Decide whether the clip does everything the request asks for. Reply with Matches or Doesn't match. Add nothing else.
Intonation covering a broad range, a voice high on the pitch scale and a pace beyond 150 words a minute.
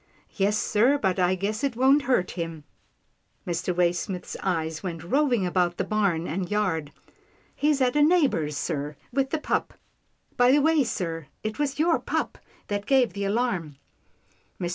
Matches